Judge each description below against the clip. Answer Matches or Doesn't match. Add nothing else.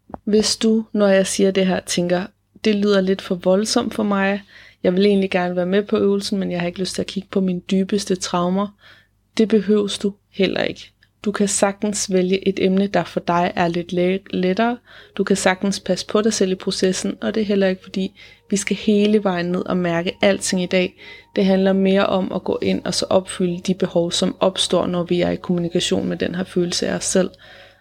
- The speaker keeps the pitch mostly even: Matches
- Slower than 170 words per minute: Doesn't match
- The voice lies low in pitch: Doesn't match